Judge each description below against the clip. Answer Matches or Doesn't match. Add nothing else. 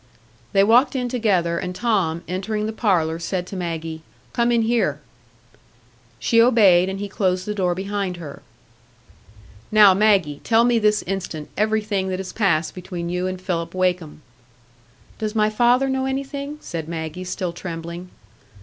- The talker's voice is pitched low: Doesn't match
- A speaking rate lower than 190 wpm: Matches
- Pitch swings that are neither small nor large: Matches